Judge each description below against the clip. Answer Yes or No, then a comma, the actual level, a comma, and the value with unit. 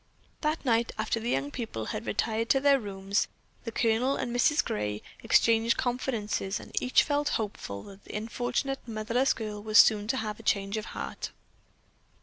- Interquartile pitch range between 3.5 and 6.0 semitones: No, average, 3.1 semitones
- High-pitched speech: Yes, high, 225 Hz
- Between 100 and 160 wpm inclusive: No, average, 170 wpm